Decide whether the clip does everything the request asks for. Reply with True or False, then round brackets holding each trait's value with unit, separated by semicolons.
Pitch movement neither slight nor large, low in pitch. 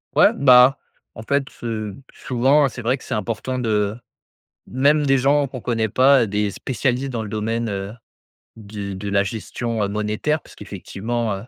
True (3.7 semitones; 115 Hz)